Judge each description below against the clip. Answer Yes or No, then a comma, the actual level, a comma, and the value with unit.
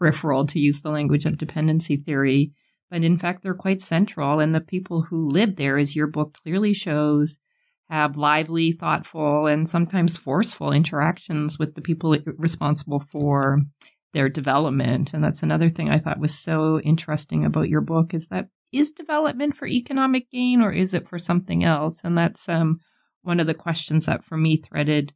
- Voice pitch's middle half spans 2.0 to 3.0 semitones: Yes, narrow, 2.6 semitones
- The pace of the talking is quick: No, average, 180 wpm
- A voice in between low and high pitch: Yes, medium, 160 Hz